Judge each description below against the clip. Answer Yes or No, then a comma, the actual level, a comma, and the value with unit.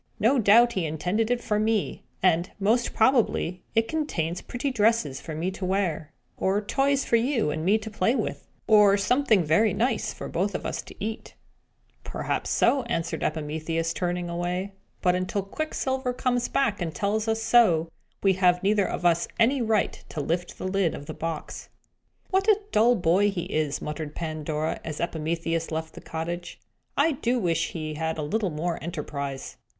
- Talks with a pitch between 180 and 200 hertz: Yes, high, 190 Hz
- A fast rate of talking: No, average, 175 wpm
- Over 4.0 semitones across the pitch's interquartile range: Yes, wide, 5.5 semitones